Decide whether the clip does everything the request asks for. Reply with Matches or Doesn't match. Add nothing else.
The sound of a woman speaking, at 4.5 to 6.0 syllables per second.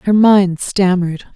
Doesn't match